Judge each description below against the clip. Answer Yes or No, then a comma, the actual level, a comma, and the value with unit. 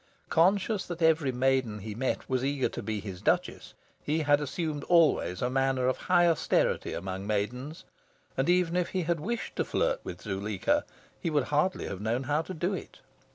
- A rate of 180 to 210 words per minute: Yes, average, 190 wpm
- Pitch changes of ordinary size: No, wide, 5.8 semitones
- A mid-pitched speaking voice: Yes, medium, 145 Hz